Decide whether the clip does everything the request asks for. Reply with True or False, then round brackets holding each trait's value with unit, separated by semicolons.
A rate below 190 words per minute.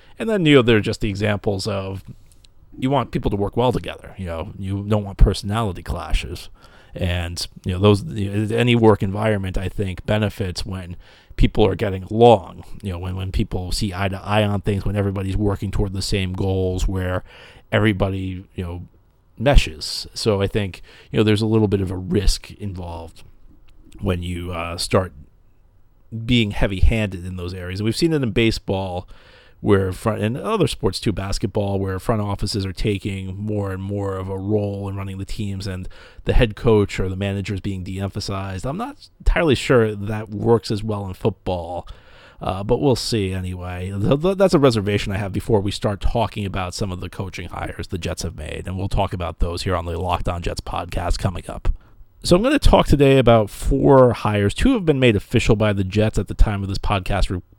False (205 wpm)